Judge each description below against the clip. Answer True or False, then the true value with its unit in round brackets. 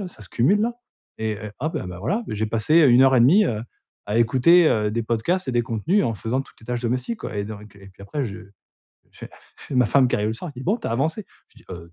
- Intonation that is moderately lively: False (6.4 semitones)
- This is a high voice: False (120 Hz)